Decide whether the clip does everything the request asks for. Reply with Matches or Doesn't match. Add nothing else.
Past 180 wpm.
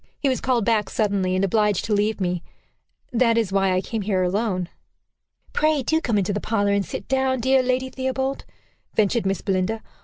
Matches